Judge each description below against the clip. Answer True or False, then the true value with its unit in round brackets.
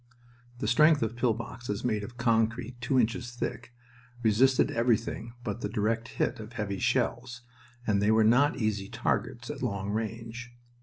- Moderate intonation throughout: False (2.1 semitones)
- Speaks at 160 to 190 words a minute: True (165 wpm)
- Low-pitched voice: True (115 Hz)